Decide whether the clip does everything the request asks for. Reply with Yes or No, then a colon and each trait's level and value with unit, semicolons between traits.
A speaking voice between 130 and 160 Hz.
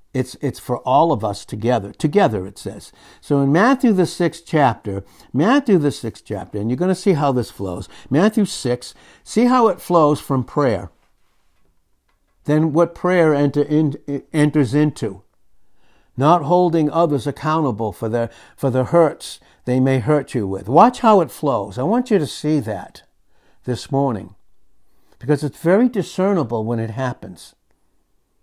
Yes: medium, 140 Hz